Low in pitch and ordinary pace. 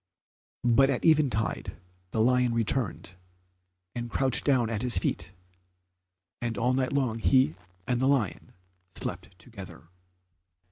No: low, 120 Hz; slow, 125 wpm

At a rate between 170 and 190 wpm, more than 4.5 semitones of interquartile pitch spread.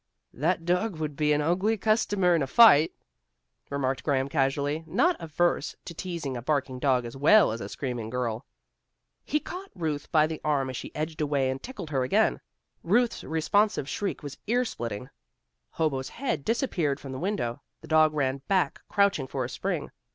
Yes: average, 180 wpm; average, 5.1 semitones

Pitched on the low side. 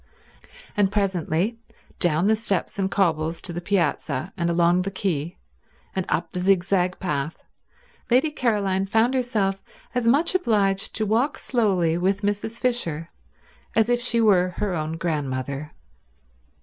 No: high, 195 Hz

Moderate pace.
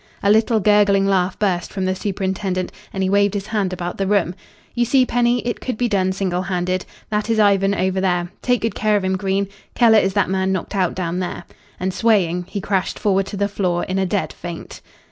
No: fast, 220 wpm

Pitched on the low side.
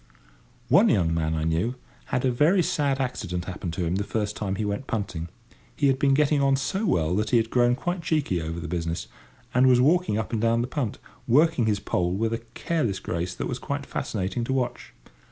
Yes: low, 115 Hz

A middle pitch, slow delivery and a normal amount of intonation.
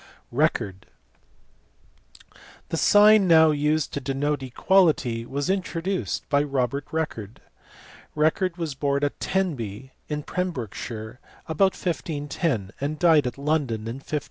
Yes: medium, 145 Hz; slow, 120 wpm; average, 4.3 semitones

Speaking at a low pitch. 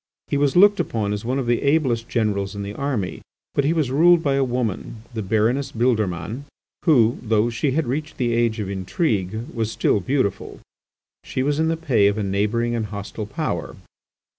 Yes: low, 120 Hz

